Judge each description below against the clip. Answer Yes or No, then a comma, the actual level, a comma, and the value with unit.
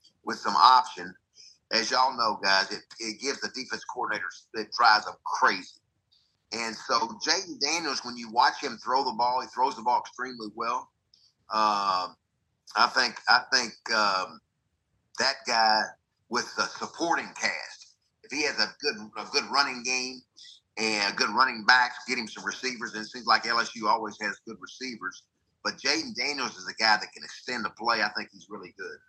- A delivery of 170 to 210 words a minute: Yes, average, 180 wpm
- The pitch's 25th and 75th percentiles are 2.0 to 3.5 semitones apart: Yes, average, 3.0 semitones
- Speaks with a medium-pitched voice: No, low, 120 Hz